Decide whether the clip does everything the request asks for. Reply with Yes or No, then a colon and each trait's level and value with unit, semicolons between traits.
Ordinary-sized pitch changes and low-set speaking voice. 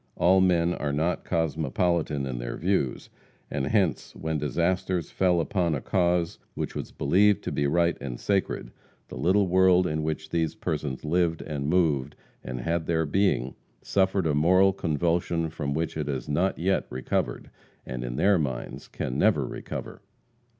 Yes: average, 3.8 semitones; very low, 80 Hz